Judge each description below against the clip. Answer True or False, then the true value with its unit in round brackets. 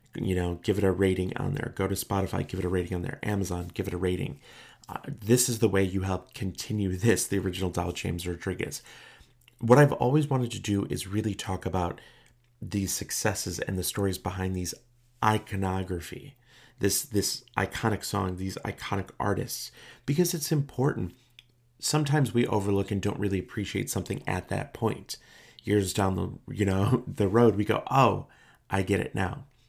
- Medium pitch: False (100 Hz)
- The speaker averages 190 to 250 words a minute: False (180 wpm)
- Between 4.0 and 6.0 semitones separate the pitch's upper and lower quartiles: True (4.3 semitones)